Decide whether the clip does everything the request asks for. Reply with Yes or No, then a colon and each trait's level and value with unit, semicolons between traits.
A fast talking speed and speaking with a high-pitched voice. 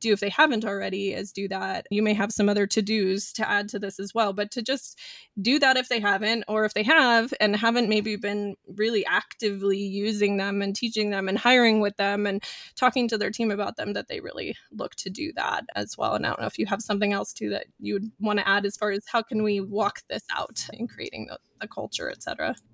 Yes: fast, 250 wpm; high, 210 Hz